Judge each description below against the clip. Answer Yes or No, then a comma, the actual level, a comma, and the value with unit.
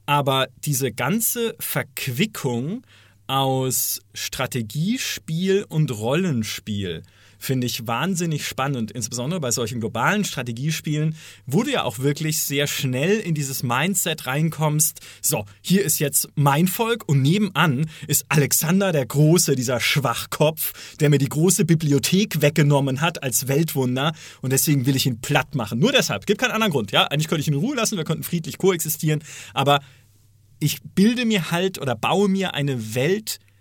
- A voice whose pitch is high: No, medium, 145 Hz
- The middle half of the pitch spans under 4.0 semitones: No, average, 5.0 semitones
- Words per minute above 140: Yes, average, 155 wpm